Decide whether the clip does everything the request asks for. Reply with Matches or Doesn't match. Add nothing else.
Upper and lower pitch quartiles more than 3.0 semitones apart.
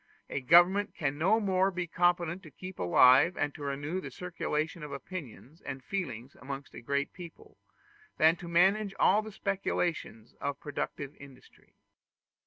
Matches